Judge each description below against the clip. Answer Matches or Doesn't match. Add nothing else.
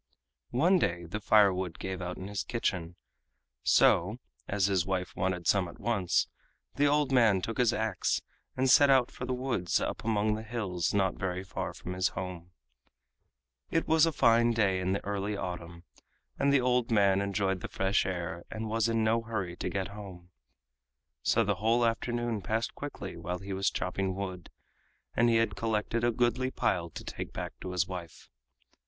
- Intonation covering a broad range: Doesn't match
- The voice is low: Matches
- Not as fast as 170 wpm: Doesn't match